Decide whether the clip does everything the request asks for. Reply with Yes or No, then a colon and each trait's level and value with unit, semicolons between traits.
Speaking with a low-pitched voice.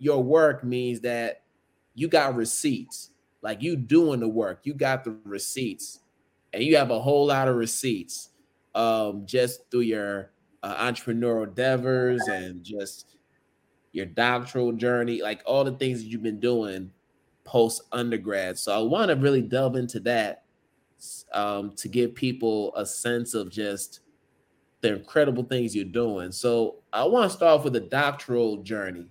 Yes: low, 120 Hz